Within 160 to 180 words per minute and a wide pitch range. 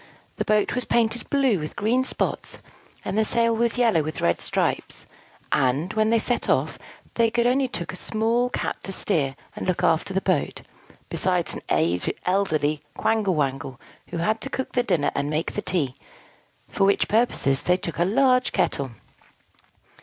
Yes: average, 170 wpm; wide, 7.1 semitones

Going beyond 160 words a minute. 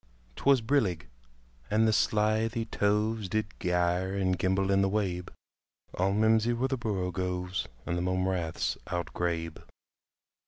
No: average, 140 wpm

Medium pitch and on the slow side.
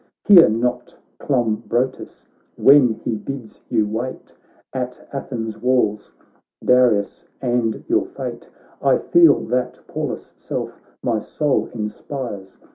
No: low, 125 Hz; slow, 110 wpm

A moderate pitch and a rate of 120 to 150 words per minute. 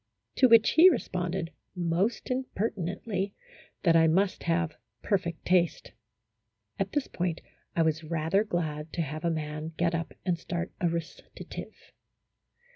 Yes: medium, 170 Hz; average, 140 wpm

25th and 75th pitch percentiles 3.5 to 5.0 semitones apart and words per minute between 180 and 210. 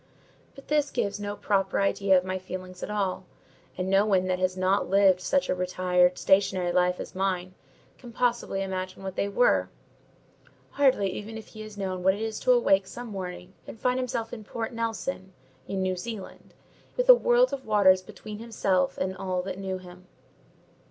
No: average, 3.1 semitones; average, 185 wpm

